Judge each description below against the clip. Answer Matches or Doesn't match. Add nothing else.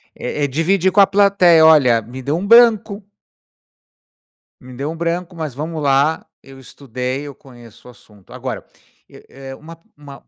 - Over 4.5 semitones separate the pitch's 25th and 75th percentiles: Matches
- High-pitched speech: Doesn't match